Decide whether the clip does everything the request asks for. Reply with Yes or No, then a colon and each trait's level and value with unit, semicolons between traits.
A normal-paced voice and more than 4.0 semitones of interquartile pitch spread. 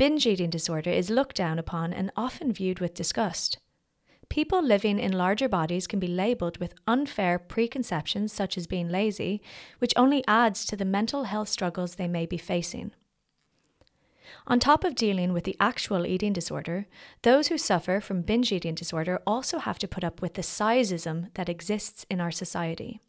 Yes: average, 175 wpm; average, 4.7 semitones